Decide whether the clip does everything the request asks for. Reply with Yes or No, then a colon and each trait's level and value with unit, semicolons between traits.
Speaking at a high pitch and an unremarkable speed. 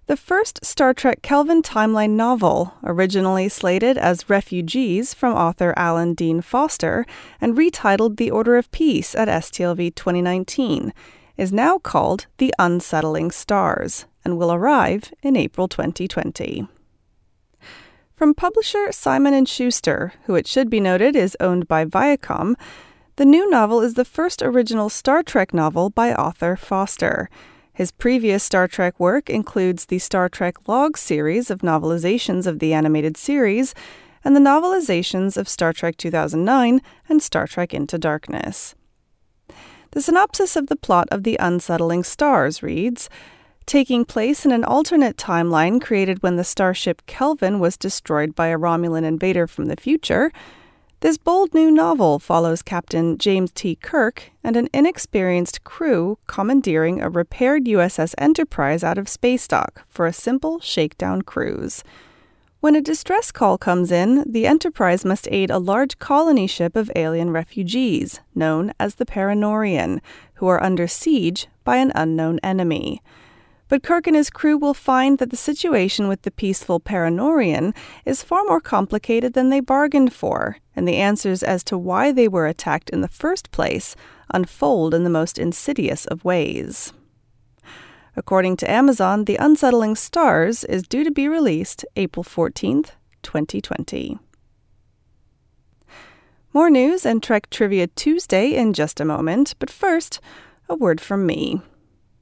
Yes: high, 205 Hz; average, 145 wpm